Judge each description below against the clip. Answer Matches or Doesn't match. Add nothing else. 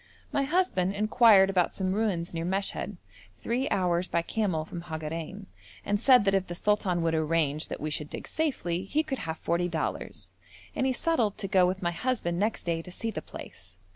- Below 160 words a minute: Doesn't match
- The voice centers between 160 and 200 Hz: Matches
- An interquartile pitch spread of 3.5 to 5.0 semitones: Matches